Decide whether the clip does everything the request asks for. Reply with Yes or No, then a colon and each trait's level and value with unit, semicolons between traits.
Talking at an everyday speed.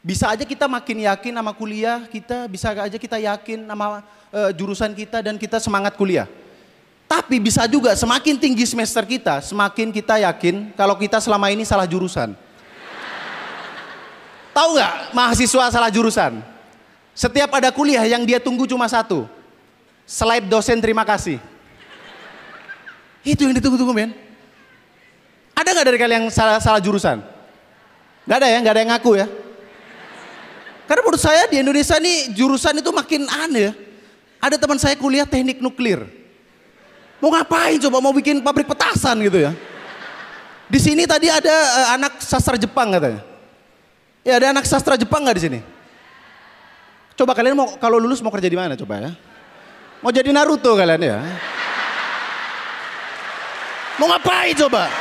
No: fast, 145 wpm